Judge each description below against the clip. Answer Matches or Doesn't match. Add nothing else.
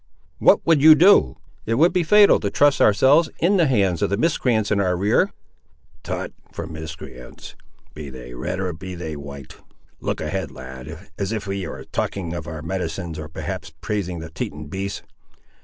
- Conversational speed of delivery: Matches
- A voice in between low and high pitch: Doesn't match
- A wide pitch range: Matches